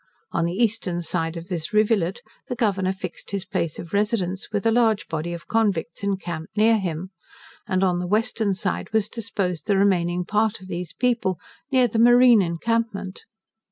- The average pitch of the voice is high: Yes, high, 195 Hz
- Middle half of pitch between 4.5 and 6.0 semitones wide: No, average, 4.0 semitones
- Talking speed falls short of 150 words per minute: No, average, 175 wpm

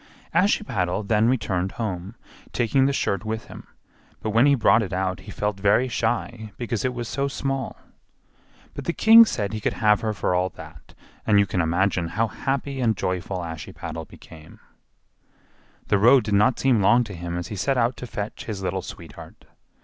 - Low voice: Yes, low, 105 Hz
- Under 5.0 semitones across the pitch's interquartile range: Yes, average, 4.3 semitones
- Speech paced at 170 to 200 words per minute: Yes, average, 190 wpm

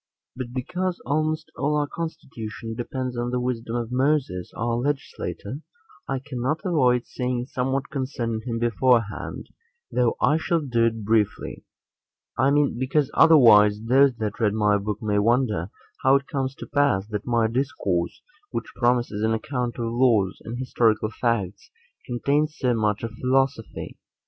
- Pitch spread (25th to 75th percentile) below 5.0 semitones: Yes, average, 3.2 semitones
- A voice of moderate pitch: No, low, 120 Hz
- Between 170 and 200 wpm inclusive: No, average, 155 wpm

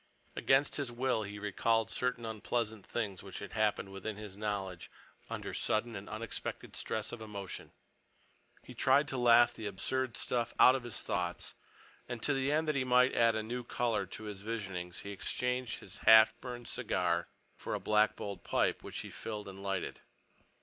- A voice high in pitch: No, low, 110 Hz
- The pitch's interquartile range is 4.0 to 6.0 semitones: No, average, 3.2 semitones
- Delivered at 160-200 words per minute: Yes, average, 180 wpm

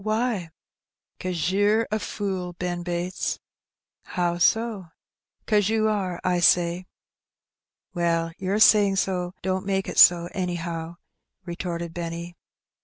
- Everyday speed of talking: No, slow, 115 wpm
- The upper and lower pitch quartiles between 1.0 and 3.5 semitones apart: Yes, narrow, 2.6 semitones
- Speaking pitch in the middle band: Yes, medium, 180 Hz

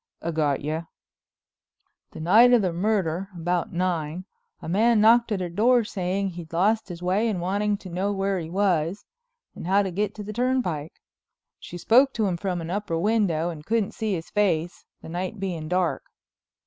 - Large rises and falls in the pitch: No, average, 3.6 semitones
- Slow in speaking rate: No, average, 185 wpm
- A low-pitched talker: No, medium, 185 Hz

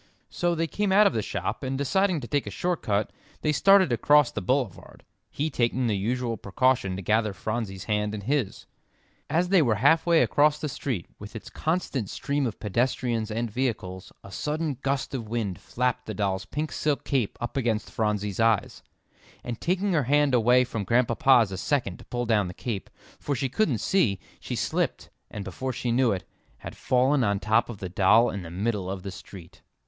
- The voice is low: Yes, low, 120 Hz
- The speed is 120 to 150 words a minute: No, average, 195 wpm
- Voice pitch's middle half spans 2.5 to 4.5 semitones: No, wide, 5.4 semitones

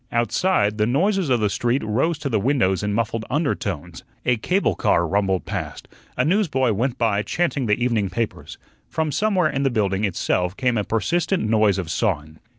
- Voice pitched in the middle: No, low, 115 Hz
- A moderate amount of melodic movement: No, wide, 5.8 semitones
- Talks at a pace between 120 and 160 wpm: No, average, 180 wpm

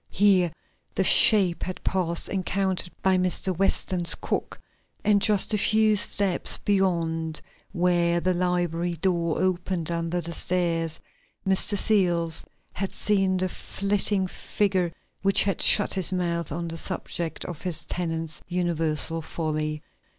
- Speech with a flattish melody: Yes, narrow, 2.3 semitones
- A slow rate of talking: Yes, slow, 130 wpm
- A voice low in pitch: No, medium, 180 Hz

